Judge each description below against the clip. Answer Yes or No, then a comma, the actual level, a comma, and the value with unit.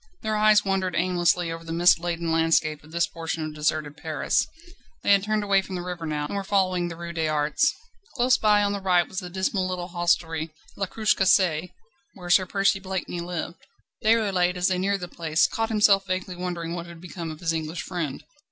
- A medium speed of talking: No, fast, 210 wpm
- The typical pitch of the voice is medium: Yes, medium, 180 Hz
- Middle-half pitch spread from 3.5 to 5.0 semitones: No, average, 2.7 semitones